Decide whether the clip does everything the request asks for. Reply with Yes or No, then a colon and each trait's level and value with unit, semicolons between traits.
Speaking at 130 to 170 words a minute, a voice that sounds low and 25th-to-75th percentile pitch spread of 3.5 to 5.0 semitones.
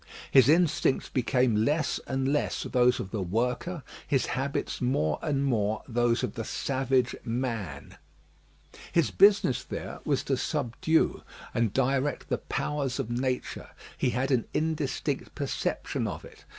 No: average, 140 wpm; low, 130 Hz; average, 3.1 semitones